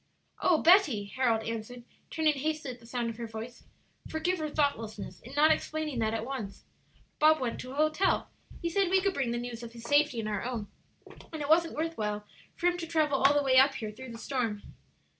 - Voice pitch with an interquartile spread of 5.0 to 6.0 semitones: Yes, average, 5.3 semitones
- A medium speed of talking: No, fast, 220 wpm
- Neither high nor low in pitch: No, very high, 260 Hz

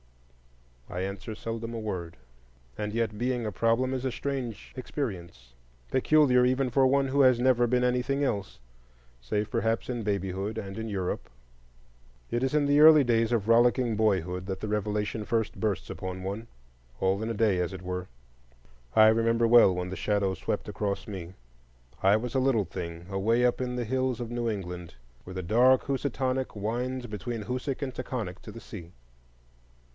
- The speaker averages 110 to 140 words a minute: No, average, 175 wpm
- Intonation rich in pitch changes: No, average, 4.5 semitones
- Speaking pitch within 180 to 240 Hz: No, low, 115 Hz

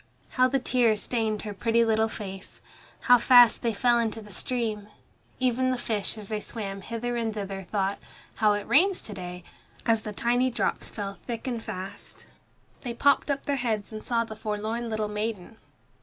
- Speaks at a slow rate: No, average, 185 wpm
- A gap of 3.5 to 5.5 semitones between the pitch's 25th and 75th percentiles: No, narrow, 2.6 semitones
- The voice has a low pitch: No, high, 225 Hz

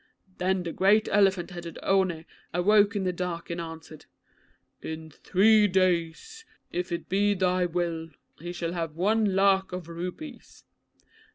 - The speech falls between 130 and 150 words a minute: Yes, average, 145 wpm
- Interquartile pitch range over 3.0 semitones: No, narrow, 2.5 semitones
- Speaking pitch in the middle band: Yes, medium, 180 Hz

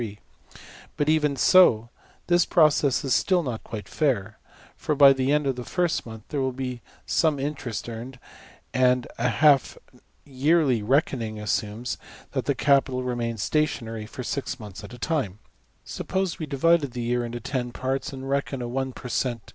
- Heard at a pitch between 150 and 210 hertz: No, low, 130 Hz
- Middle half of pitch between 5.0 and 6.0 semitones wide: No, average, 3.5 semitones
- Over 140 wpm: Yes, average, 170 wpm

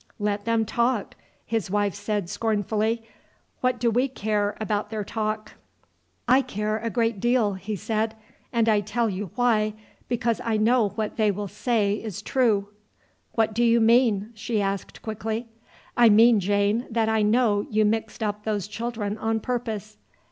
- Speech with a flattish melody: Yes, narrow, 1.9 semitones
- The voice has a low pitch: No, high, 220 Hz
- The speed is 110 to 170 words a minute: Yes, average, 160 wpm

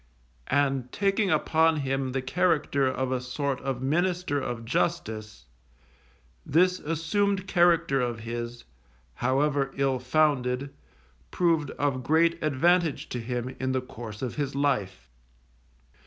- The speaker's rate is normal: No, slow, 125 wpm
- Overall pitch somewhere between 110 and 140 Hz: Yes, low, 135 Hz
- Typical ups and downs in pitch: Yes, average, 4.4 semitones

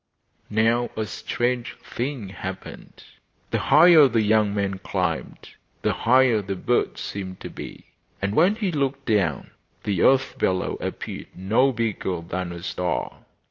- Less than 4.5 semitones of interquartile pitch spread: No, average, 5.2 semitones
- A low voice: Yes, low, 110 Hz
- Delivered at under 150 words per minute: Yes, average, 140 wpm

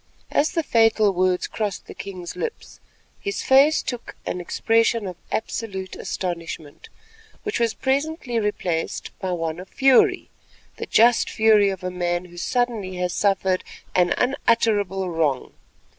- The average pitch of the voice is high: Yes, high, 200 Hz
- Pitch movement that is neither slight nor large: Yes, average, 4.7 semitones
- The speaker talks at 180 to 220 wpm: No, slow, 135 wpm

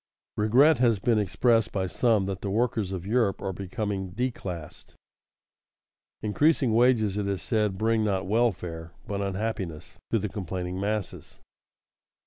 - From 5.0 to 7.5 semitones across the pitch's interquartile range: No, average, 3.2 semitones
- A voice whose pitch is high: No, low, 105 Hz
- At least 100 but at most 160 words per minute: Yes, slow, 135 wpm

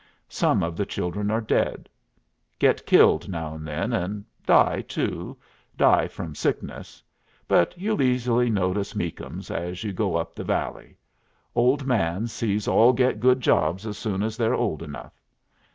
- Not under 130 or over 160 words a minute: Yes, average, 155 wpm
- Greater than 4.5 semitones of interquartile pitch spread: Yes, average, 5.3 semitones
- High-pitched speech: No, low, 105 Hz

